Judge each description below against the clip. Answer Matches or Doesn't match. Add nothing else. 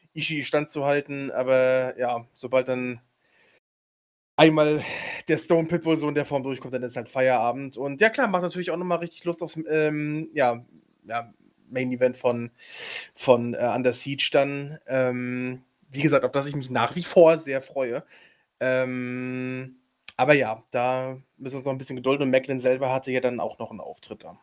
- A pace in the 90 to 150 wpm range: Doesn't match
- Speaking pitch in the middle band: Doesn't match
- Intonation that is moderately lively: Matches